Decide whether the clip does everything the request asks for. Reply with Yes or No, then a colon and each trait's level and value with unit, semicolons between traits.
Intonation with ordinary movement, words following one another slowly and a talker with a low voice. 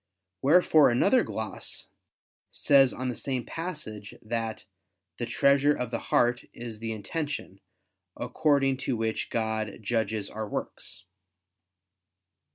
Yes: average, 4.0 semitones; slow, 115 wpm; low, 120 Hz